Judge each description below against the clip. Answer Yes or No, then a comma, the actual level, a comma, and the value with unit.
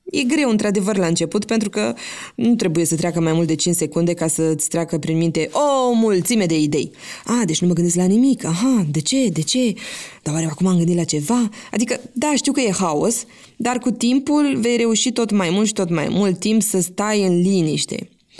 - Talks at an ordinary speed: No, fast, 220 wpm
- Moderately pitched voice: No, high, 210 Hz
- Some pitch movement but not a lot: No, wide, 6.2 semitones